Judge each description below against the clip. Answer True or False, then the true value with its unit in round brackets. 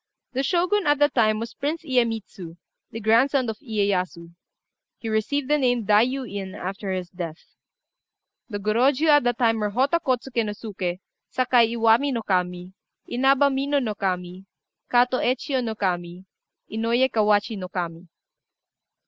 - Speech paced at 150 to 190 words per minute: True (155 wpm)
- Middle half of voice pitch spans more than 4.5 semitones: True (5.1 semitones)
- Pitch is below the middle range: False (225 Hz)